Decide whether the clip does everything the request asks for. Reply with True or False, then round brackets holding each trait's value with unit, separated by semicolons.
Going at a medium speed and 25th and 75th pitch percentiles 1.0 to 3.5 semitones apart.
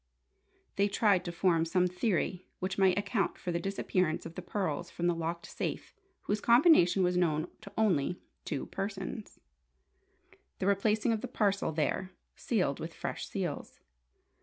True (155 wpm; 2.8 semitones)